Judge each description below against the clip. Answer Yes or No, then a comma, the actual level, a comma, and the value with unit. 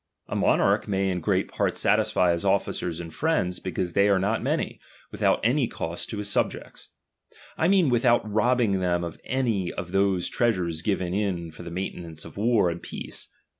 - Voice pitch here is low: Yes, very low, 95 Hz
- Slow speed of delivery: No, average, 185 wpm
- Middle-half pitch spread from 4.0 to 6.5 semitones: Yes, average, 4.4 semitones